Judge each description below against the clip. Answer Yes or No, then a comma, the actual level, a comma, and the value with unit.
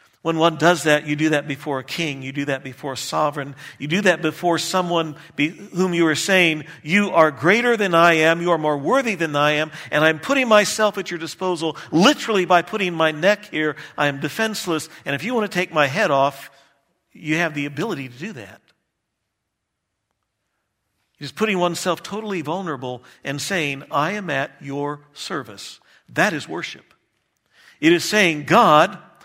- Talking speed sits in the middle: Yes, average, 185 wpm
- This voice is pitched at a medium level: Yes, medium, 165 Hz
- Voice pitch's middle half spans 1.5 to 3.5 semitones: No, average, 4.0 semitones